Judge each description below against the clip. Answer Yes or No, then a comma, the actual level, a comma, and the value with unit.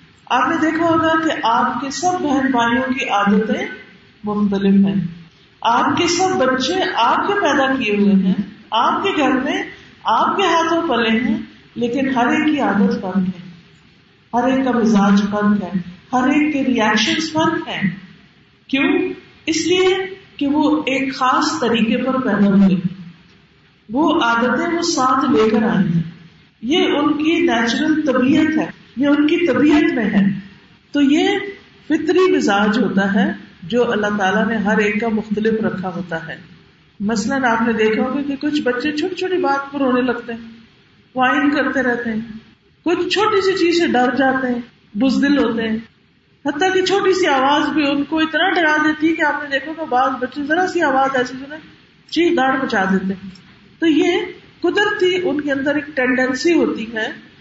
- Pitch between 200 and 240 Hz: No, very high, 260 Hz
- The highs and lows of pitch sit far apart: Yes, wide, 6.4 semitones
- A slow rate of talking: No, average, 175 wpm